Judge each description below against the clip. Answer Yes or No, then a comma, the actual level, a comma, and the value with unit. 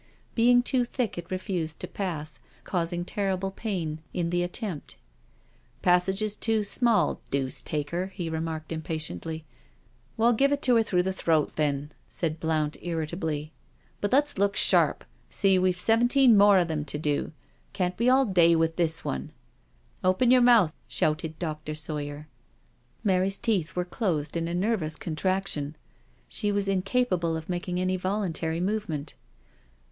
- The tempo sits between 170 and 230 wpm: No, average, 160 wpm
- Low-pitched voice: No, medium, 180 Hz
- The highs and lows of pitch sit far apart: No, average, 4.3 semitones